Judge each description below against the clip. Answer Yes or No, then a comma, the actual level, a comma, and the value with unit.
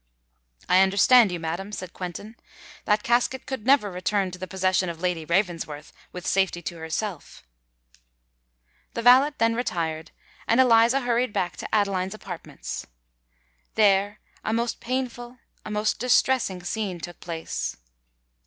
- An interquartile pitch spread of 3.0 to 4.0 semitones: No, average, 4.6 semitones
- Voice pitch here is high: Yes, high, 200 Hz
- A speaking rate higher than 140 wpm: No, slow, 135 wpm